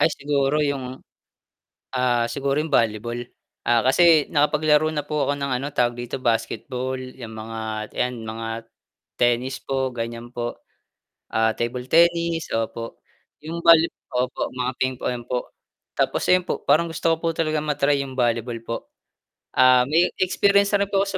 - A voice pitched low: Yes, low, 130 Hz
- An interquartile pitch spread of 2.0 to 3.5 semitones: No, average, 4.2 semitones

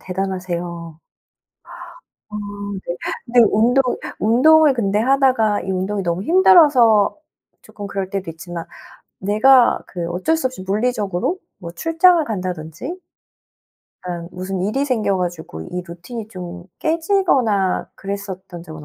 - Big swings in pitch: Yes, wide, 6.0 semitones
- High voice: Yes, high, 200 Hz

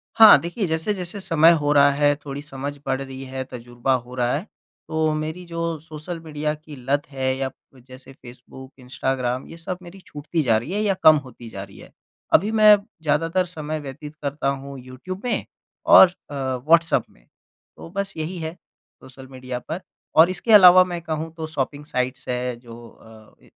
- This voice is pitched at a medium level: Yes, medium, 150 Hz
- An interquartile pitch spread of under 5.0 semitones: Yes, average, 4.2 semitones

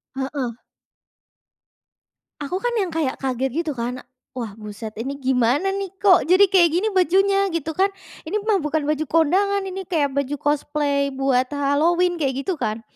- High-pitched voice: Yes, very high, 300 Hz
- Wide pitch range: Yes, wide, 5.7 semitones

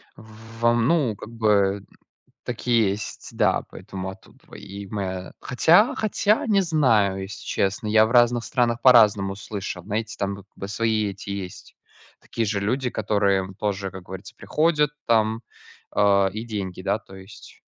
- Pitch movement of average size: Yes, average, 3.1 semitones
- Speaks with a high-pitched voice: No, low, 105 Hz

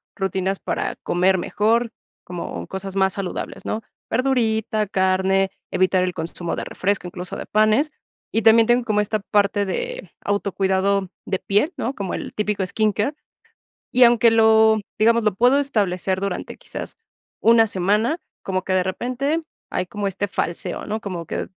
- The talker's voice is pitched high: Yes, high, 205 Hz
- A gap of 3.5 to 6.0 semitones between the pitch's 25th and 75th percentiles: No, average, 3.1 semitones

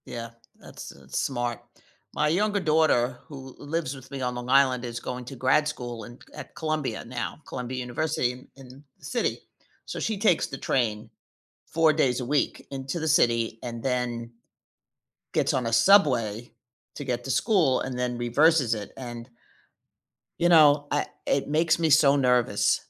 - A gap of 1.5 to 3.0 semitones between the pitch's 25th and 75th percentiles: No, average, 3.9 semitones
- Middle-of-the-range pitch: No, low, 130 Hz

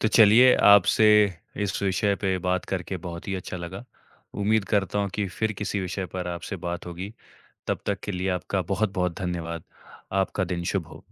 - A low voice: Yes, very low, 95 Hz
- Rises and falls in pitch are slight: Yes, narrow, 2.2 semitones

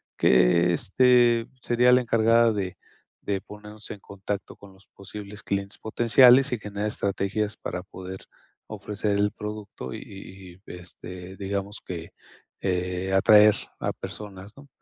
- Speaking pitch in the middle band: No, low, 100 Hz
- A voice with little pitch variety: Yes, narrow, 2.3 semitones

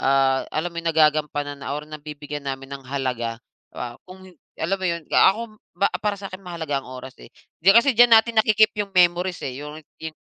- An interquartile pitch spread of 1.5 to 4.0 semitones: No, average, 5.3 semitones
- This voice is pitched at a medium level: Yes, medium, 155 Hz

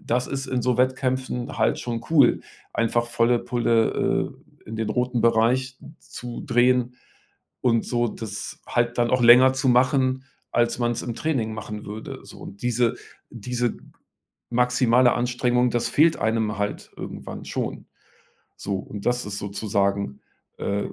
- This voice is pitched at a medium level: No, low, 120 Hz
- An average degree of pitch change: No, narrow, 1.9 semitones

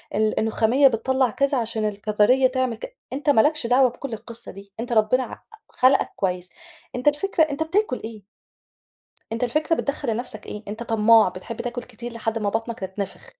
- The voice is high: Yes, high, 235 Hz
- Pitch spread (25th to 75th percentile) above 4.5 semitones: No, average, 3.5 semitones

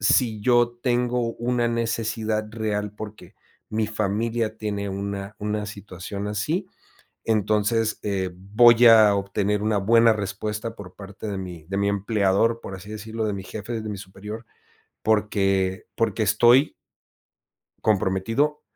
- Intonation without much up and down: Yes, narrow, 2.2 semitones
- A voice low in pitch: Yes, low, 105 Hz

